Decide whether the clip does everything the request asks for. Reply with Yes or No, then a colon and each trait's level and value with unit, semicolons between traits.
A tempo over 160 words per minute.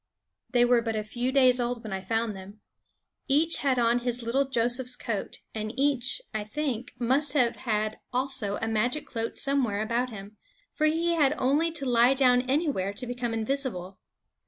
Yes: average, 180 wpm